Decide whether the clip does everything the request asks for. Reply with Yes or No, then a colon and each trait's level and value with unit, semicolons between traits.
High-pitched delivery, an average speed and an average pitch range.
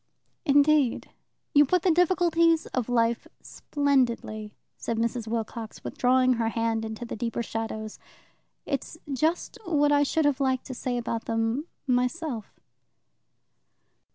No: very high, 250 Hz; slow, 130 wpm; average, 4.2 semitones